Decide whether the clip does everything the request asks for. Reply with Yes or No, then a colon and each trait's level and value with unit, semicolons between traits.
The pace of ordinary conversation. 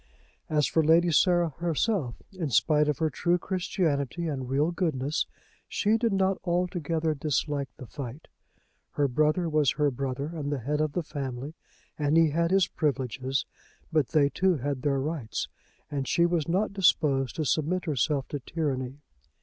Yes: average, 165 wpm